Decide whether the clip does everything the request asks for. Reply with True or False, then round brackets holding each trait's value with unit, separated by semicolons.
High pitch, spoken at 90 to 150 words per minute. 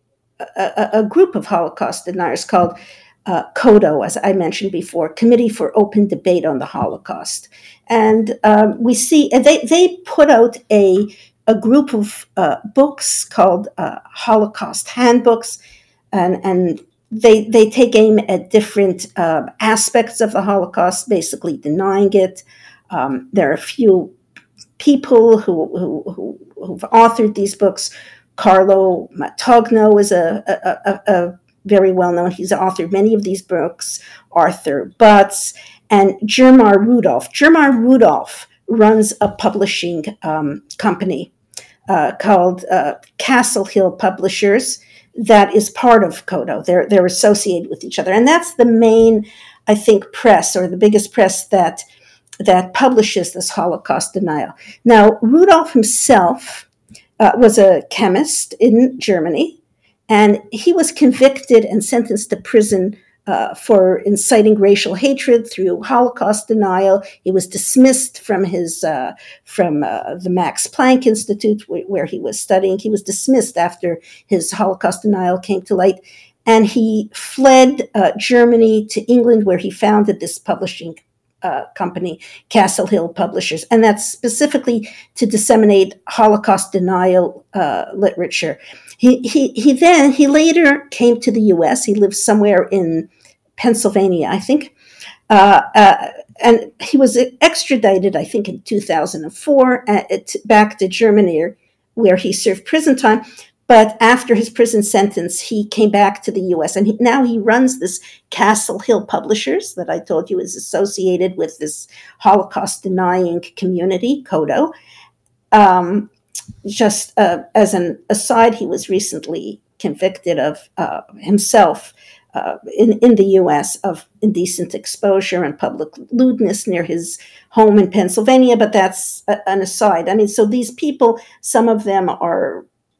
True (210 Hz; 145 wpm)